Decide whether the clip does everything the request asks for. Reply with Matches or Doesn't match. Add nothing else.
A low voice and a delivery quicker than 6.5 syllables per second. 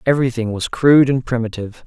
Matches